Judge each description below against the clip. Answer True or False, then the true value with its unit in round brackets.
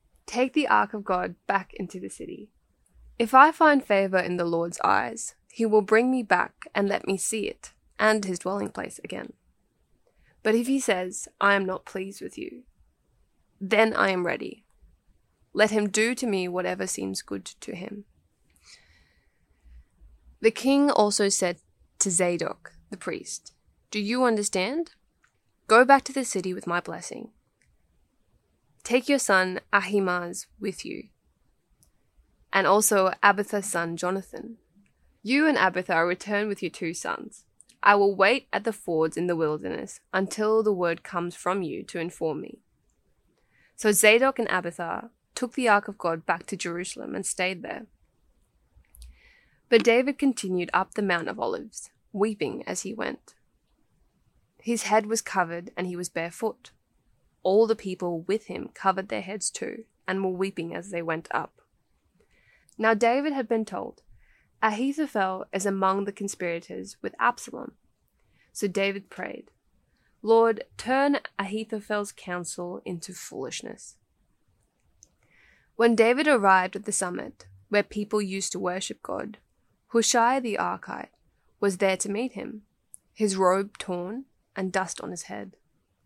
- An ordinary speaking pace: True (150 wpm)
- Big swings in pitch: False (3.8 semitones)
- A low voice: False (195 Hz)